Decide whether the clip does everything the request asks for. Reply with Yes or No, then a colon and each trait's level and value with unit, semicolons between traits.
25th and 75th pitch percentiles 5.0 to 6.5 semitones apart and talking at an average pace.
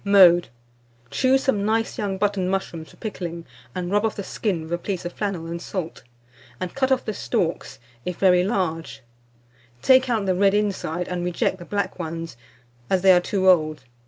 No: average, 3.0 semitones; average, 190 wpm